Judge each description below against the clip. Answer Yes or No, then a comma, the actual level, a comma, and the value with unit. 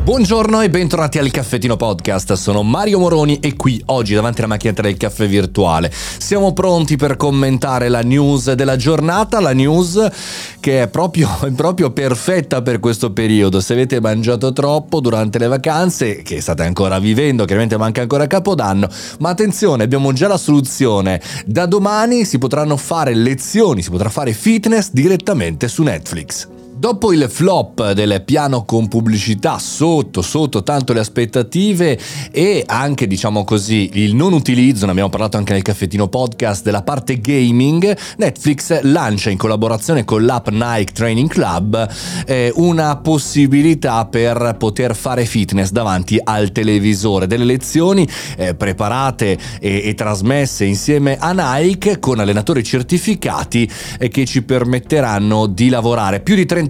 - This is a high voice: No, low, 125 Hz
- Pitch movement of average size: No, wide, 5.9 semitones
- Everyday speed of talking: Yes, average, 150 wpm